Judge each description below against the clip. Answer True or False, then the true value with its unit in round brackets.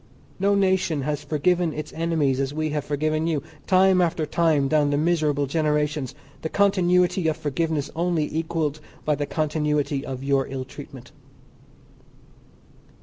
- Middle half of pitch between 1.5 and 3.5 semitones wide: True (2.6 semitones)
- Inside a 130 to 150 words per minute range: True (145 wpm)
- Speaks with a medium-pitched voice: True (155 Hz)